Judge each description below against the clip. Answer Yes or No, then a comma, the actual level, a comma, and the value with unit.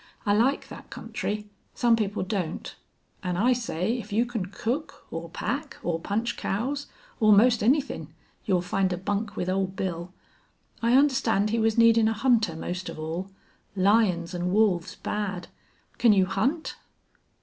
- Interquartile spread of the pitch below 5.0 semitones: Yes, average, 4.0 semitones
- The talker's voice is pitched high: Yes, high, 210 Hz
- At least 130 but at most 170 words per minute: Yes, average, 160 wpm